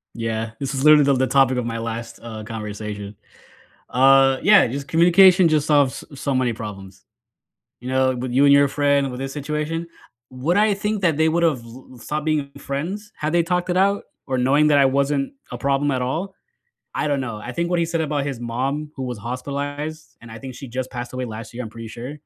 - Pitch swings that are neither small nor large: Yes, average, 3.7 semitones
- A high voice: No, low, 135 Hz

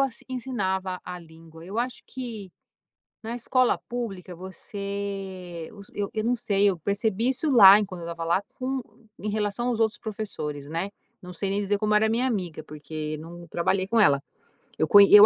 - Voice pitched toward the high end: Yes, high, 200 Hz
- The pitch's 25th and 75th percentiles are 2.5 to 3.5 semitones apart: No, average, 4.2 semitones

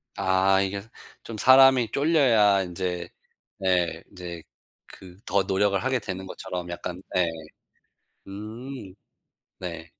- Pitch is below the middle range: Yes, very low, 95 Hz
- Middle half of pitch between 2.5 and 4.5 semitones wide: Yes, average, 3.2 semitones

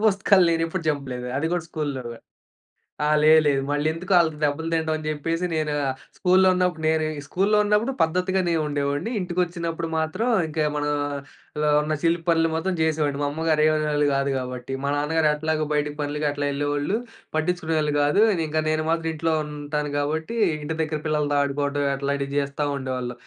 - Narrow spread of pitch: Yes, narrow, 2.2 semitones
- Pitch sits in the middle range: Yes, medium, 155 Hz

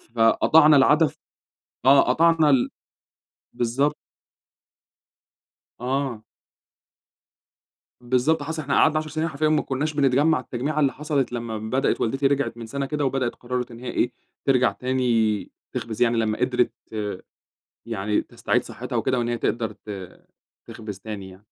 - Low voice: Yes, low, 130 Hz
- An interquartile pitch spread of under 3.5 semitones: No, average, 3.8 semitones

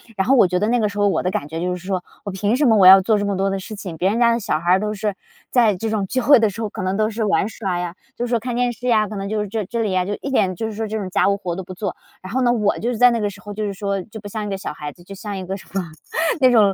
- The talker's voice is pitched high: Yes, high, 205 Hz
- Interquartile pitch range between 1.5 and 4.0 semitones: Yes, average, 2.8 semitones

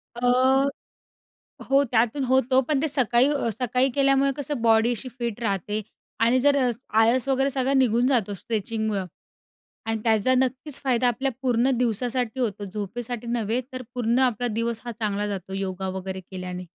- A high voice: Yes, high, 240 Hz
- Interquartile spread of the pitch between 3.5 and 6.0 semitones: No, average, 3.1 semitones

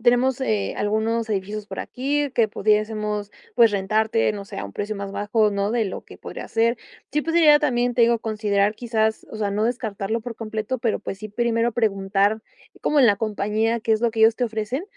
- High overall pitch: Yes, high, 220 Hz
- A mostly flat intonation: Yes, narrow, 2.3 semitones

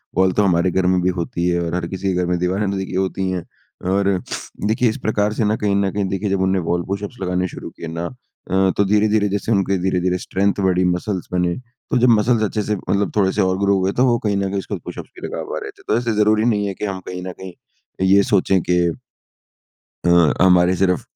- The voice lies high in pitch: No, very low, 95 Hz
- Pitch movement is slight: Yes, narrow, 2.3 semitones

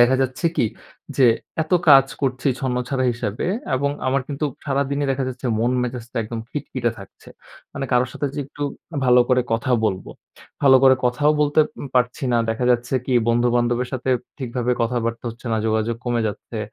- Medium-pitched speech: No, low, 125 Hz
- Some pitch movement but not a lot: No, narrow, 2.2 semitones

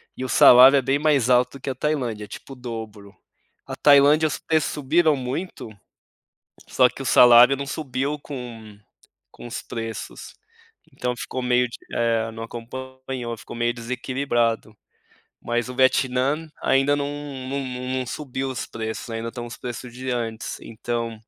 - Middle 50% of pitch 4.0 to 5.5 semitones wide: No, narrow, 2.5 semitones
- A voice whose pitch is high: No, low, 125 Hz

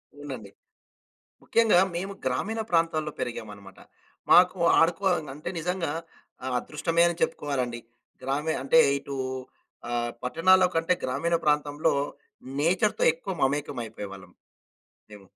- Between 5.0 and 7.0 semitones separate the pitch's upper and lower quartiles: Yes, average, 5.3 semitones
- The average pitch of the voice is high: No, medium, 150 Hz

